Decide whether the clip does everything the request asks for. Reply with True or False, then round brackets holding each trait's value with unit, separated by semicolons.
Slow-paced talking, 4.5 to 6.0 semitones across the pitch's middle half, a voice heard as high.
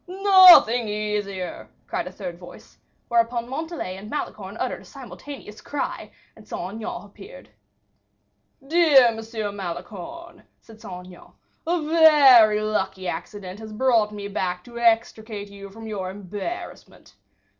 True (130 wpm; 4.9 semitones; 220 Hz)